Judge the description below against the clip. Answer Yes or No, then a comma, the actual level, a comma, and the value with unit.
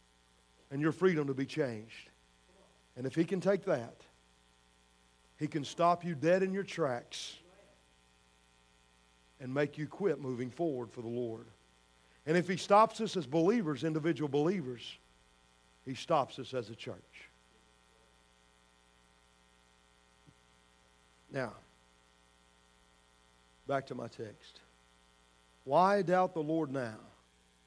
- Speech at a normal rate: No, slow, 115 wpm